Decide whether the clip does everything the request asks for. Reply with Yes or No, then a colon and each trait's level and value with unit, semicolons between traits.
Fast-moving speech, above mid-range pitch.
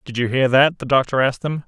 No: fast, 285 wpm; low, 135 Hz